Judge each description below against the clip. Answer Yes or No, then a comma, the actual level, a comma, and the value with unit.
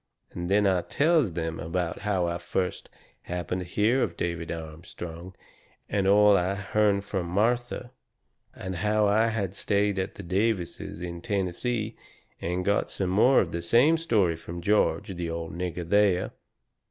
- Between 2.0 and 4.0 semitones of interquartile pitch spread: Yes, average, 3.3 semitones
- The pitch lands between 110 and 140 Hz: No, very low, 95 Hz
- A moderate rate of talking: Yes, average, 160 wpm